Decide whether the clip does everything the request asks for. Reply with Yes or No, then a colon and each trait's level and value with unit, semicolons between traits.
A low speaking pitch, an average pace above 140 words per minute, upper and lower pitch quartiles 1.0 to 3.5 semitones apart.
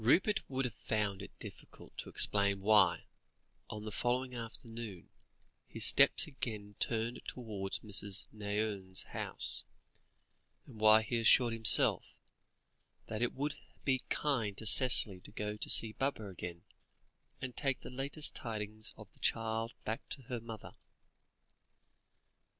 No: low, 110 Hz; slow, 135 wpm; average, 2.9 semitones